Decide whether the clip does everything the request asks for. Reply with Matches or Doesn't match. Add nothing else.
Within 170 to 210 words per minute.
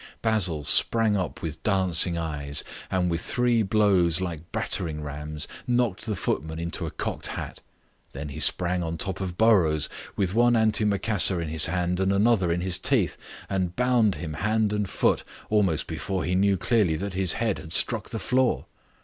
Matches